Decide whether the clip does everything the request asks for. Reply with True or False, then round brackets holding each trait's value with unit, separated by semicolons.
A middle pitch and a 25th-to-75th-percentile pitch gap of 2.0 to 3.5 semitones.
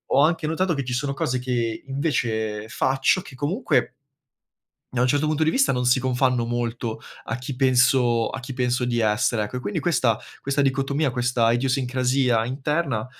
False (125 Hz; 2.5 semitones)